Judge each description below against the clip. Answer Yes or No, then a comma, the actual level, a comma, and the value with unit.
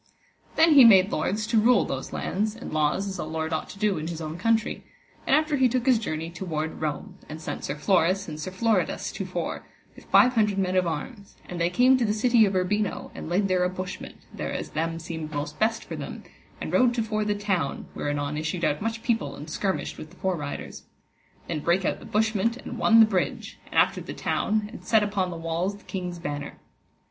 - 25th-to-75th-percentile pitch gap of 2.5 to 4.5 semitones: No, average, 5.2 semitones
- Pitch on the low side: No, high, 190 Hz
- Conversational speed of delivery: No, fast, 225 wpm